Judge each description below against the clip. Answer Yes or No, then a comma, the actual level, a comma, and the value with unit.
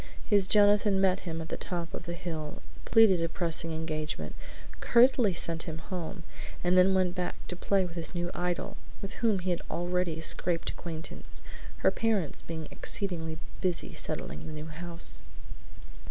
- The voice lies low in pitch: No, medium, 175 Hz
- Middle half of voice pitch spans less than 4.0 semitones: Yes, average, 2.7 semitones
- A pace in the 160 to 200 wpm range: Yes, average, 165 wpm